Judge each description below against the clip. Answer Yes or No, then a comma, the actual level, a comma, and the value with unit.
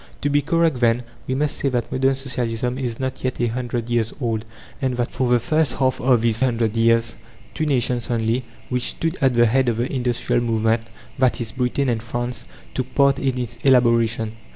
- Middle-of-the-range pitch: No, low, 125 Hz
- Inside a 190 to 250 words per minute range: Yes, average, 200 wpm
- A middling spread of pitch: No, narrow, 2.2 semitones